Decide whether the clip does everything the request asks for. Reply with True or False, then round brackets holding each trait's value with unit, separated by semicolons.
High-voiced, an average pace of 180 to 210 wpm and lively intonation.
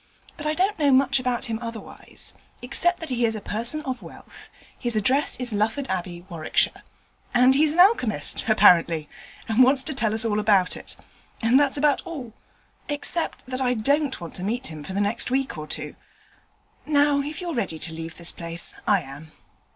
True (240 Hz; 190 wpm; 6.1 semitones)